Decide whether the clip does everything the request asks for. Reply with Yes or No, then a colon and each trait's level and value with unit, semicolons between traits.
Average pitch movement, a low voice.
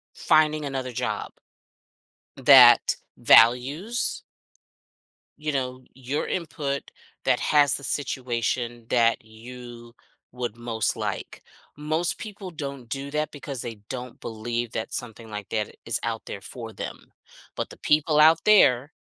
Yes: average, 4.2 semitones; low, 125 Hz